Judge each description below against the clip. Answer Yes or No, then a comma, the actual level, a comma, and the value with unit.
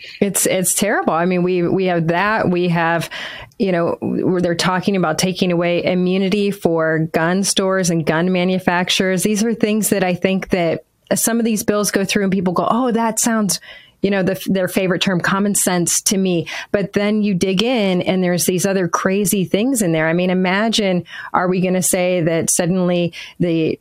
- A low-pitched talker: No, medium, 185 Hz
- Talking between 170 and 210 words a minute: Yes, average, 200 wpm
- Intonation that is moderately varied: No, narrow, 2.3 semitones